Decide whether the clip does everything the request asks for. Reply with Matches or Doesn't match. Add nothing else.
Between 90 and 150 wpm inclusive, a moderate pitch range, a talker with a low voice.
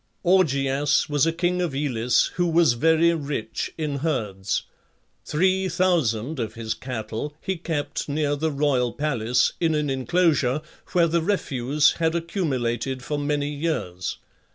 Doesn't match